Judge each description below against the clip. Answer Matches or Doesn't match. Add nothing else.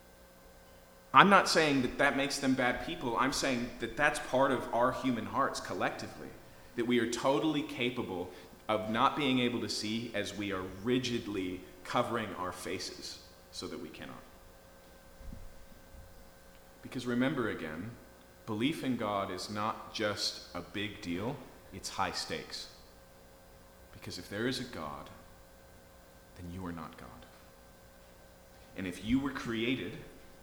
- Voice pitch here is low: Matches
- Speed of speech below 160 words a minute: Matches